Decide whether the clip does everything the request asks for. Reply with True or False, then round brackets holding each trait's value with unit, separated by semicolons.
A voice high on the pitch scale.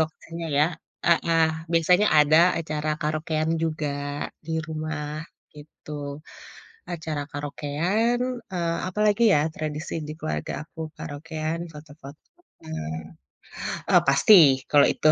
False (155 Hz)